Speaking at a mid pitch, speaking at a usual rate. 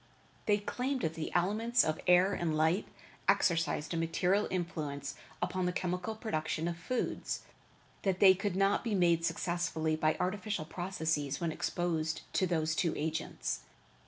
Yes: medium, 175 Hz; average, 150 wpm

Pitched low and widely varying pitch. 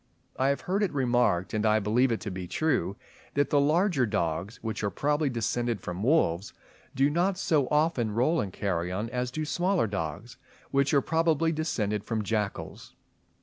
Yes: low, 120 Hz; wide, 6.5 semitones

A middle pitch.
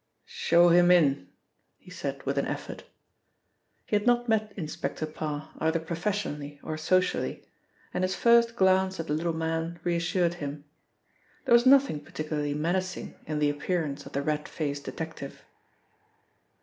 Yes: medium, 165 Hz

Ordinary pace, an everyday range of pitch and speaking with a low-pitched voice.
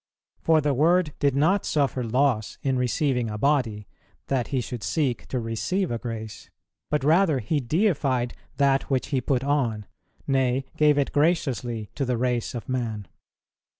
Yes: average, 160 wpm; average, 3.5 semitones; low, 130 Hz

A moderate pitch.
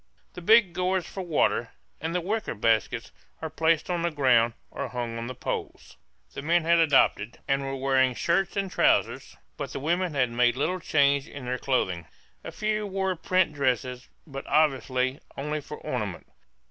Yes: medium, 145 Hz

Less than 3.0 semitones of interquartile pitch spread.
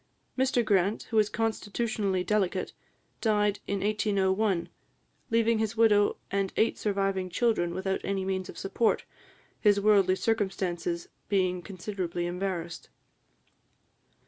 Yes: narrow, 2.5 semitones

